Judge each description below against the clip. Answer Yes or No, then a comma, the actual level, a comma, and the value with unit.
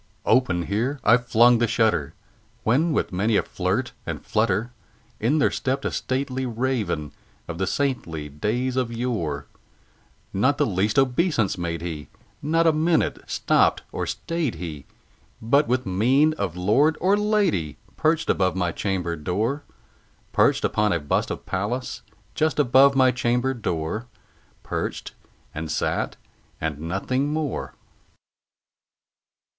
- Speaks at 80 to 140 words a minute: Yes, slow, 135 wpm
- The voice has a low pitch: Yes, low, 115 Hz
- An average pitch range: No, wide, 6.9 semitones